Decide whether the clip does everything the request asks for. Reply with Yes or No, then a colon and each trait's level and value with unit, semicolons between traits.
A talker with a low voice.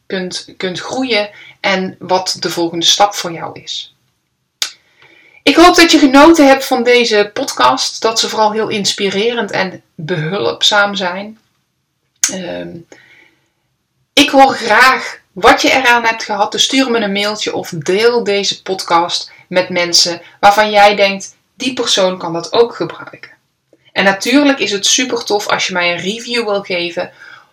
No: high, 205 Hz